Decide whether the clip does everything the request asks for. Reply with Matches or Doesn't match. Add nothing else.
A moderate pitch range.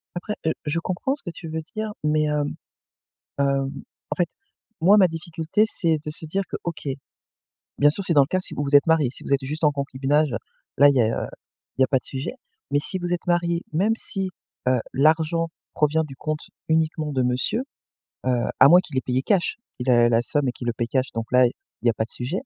Matches